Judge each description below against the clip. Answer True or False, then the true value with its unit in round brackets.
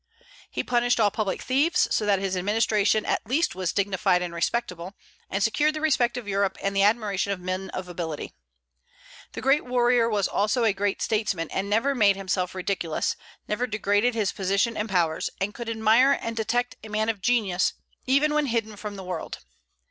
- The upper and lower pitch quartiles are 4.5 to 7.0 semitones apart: False (3.7 semitones)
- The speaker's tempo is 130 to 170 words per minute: False (185 wpm)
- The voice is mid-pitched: False (210 Hz)